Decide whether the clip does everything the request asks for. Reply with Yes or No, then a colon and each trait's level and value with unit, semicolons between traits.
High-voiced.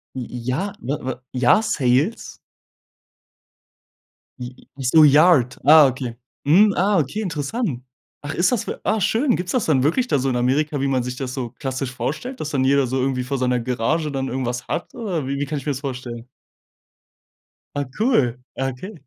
No: medium, 140 Hz